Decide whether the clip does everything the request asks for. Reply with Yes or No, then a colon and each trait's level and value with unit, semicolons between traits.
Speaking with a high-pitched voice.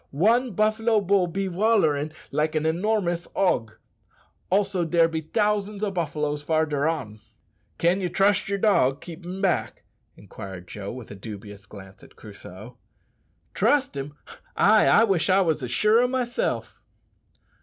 No: medium, 170 Hz